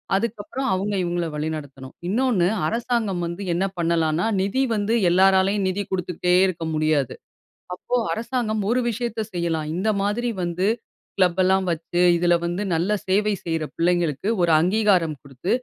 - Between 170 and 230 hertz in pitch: Yes, medium, 185 Hz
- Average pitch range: Yes, average, 3.6 semitones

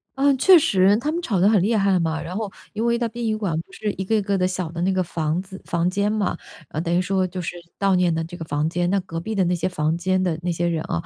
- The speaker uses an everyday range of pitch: Yes, average, 3.4 semitones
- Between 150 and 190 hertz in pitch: Yes, medium, 185 Hz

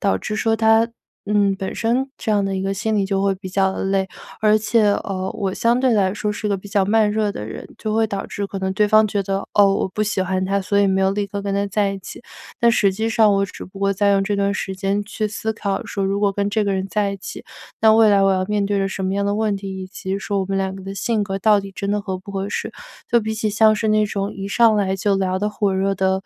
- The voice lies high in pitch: Yes, high, 200 Hz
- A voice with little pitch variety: Yes, narrow, 1.6 semitones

